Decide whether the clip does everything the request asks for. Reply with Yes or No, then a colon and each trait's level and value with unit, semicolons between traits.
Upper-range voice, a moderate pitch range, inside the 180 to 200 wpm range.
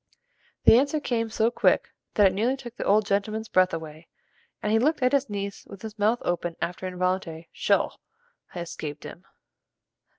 Yes: high, 205 Hz; average, 4.0 semitones; average, 185 wpm